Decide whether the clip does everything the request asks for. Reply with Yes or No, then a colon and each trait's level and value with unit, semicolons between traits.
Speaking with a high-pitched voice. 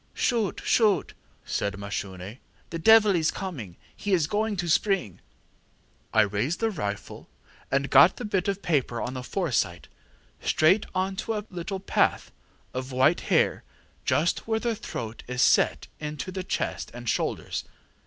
No: medium, 165 Hz